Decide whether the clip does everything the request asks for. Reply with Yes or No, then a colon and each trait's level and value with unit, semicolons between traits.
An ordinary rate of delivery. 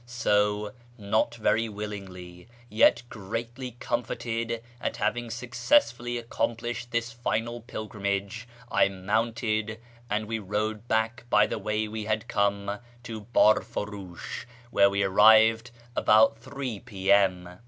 No: slow, 120 wpm